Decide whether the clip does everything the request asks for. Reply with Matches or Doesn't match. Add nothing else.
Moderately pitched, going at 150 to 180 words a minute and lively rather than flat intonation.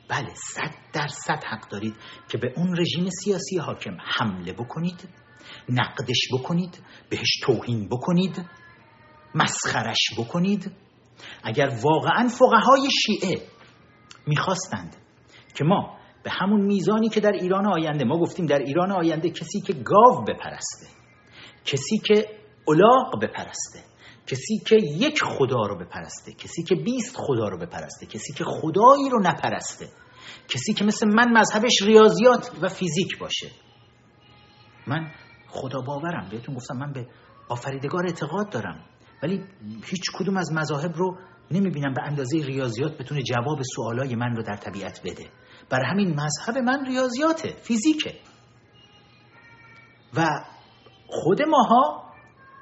Doesn't match